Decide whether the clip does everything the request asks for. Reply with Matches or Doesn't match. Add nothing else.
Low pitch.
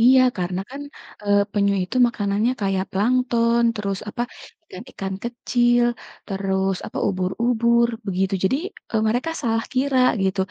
Doesn't match